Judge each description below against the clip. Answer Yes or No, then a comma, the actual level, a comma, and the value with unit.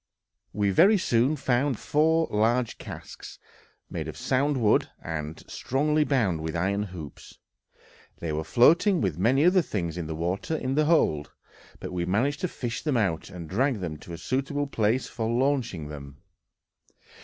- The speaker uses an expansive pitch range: Yes, wide, 8.5 semitones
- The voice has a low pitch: Yes, low, 115 Hz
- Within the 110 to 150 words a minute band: No, average, 165 wpm